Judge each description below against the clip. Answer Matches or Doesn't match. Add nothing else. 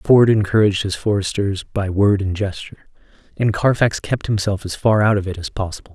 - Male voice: Matches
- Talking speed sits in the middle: Matches